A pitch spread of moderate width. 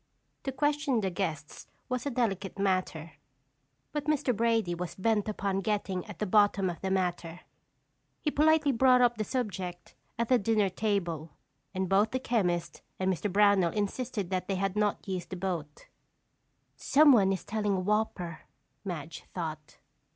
Yes: average, 3.9 semitones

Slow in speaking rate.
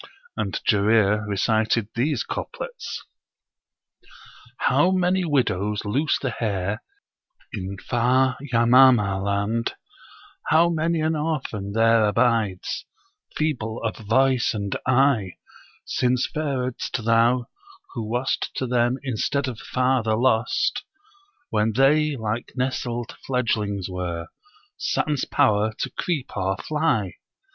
Yes: slow, 105 wpm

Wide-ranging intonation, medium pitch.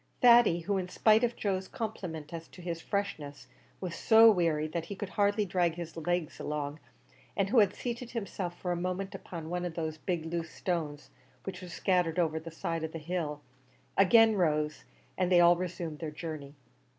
No: average, 3.4 semitones; medium, 175 Hz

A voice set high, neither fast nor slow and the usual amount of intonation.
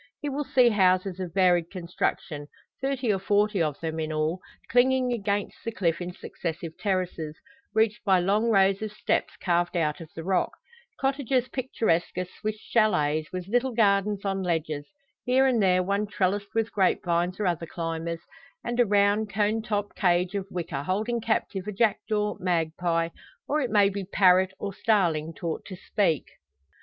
Yes: high, 195 Hz; average, 170 wpm; average, 3.8 semitones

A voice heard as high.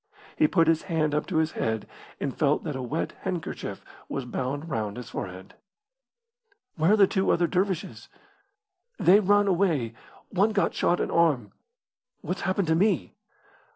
No: medium, 165 Hz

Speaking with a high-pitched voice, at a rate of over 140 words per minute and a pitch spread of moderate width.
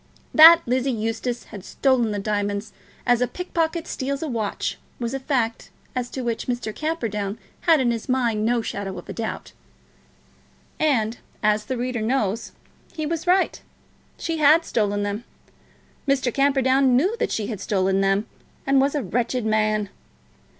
Yes: high, 240 Hz; average, 160 wpm; average, 4.3 semitones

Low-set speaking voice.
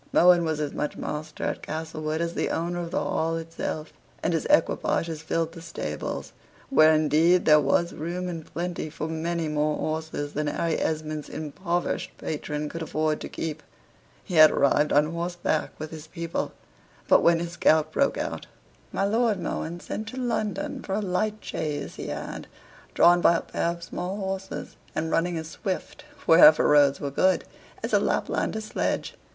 No: medium, 165 Hz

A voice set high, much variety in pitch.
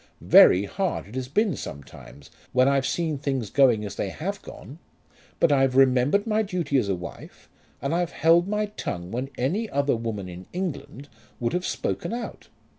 No: low, 135 Hz; wide, 7.5 semitones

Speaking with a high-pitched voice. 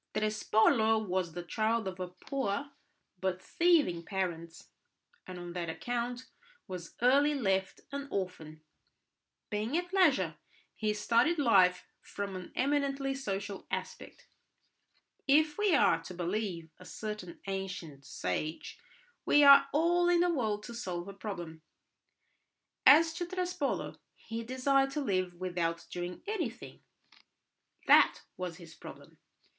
Yes: high, 210 Hz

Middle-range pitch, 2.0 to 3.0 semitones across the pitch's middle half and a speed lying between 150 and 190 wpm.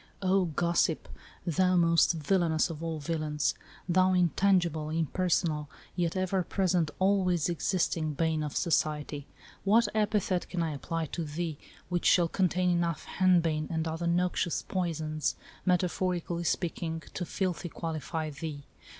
No: medium, 170 Hz; narrow, 2.4 semitones; slow, 135 wpm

